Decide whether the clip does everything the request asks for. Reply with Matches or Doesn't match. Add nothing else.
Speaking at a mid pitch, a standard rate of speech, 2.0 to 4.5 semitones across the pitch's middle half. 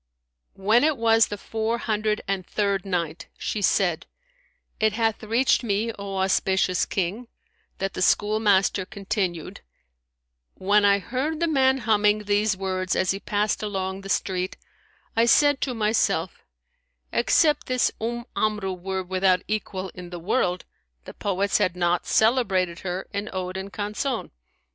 Doesn't match